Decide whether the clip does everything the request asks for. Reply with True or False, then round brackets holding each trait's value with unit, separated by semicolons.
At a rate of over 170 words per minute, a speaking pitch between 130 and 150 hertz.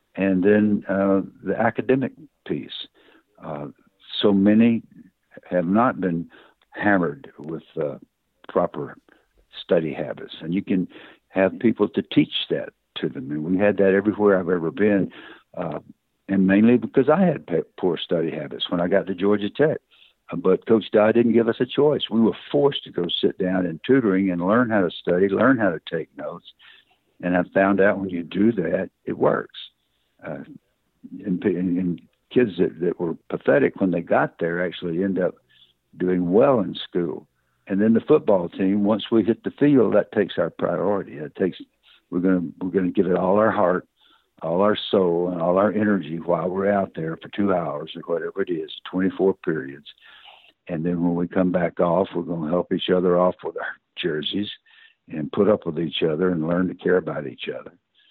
False (190 wpm; 95 Hz)